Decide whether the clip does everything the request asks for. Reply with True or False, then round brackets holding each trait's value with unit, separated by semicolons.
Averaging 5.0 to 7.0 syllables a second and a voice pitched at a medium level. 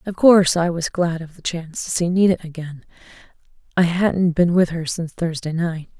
True (5.4 syllables/s; 170 Hz)